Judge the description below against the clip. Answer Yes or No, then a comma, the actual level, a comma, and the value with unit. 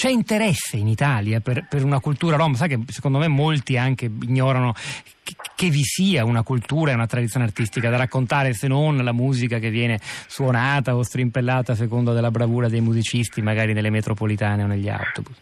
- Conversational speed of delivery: No, fast, 190 wpm